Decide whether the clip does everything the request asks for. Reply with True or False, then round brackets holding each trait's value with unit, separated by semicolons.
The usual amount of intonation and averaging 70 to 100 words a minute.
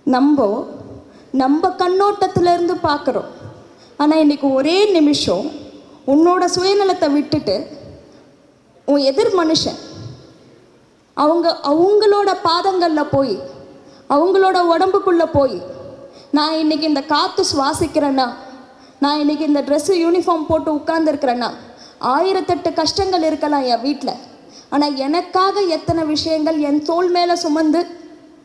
True (3.6 semitones; 95 wpm)